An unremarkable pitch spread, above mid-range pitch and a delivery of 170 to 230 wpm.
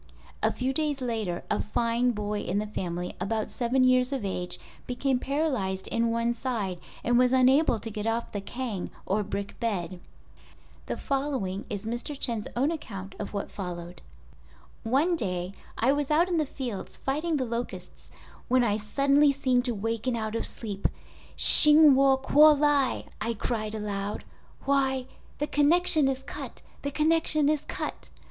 No: average, 4.9 semitones; high, 245 Hz; average, 160 wpm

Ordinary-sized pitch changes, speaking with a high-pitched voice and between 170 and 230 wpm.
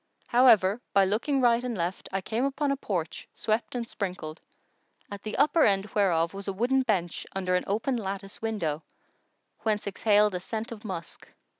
Yes: average, 3.7 semitones; high, 210 Hz; average, 175 wpm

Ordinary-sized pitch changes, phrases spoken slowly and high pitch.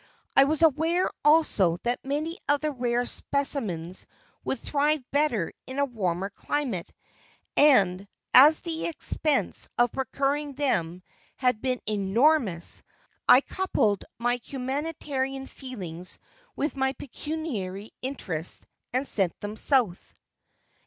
No: wide, 6.3 semitones; slow, 115 wpm; very high, 260 Hz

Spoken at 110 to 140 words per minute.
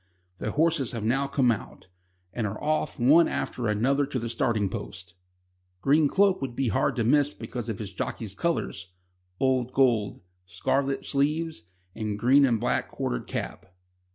No: average, 160 wpm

